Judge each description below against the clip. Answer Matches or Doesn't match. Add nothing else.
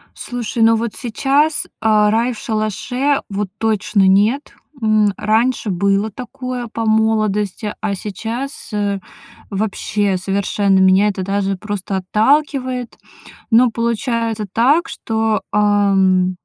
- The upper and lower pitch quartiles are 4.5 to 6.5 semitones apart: Doesn't match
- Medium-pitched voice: Doesn't match